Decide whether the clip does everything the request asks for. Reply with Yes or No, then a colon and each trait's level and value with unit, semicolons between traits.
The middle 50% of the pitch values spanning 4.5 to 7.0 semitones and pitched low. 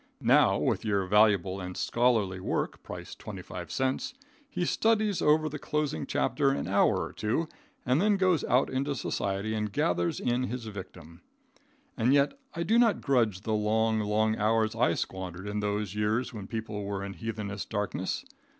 Yes: average, 5.1 semitones; low, 110 Hz